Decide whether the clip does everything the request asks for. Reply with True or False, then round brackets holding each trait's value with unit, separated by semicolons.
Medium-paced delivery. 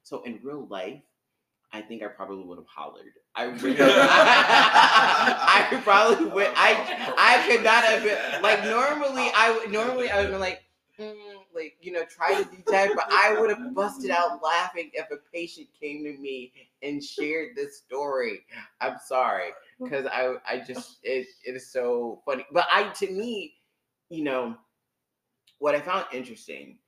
True (175 wpm)